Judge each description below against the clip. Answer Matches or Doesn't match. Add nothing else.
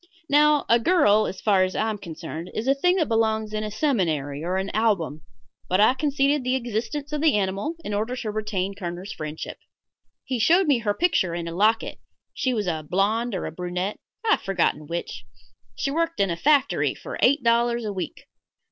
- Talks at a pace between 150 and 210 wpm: Matches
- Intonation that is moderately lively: Doesn't match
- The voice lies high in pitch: Matches